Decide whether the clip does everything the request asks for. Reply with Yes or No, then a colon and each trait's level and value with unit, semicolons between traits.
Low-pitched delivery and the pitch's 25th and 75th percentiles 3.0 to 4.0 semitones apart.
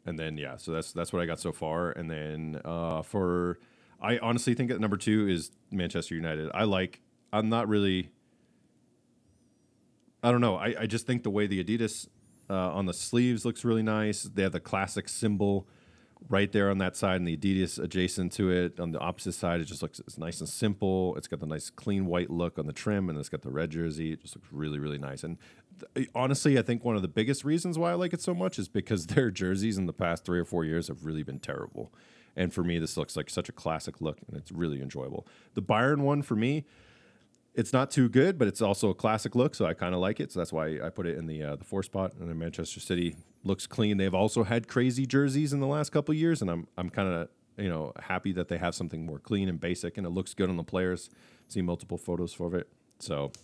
No: very low, 95 Hz; average, 4.7 semitones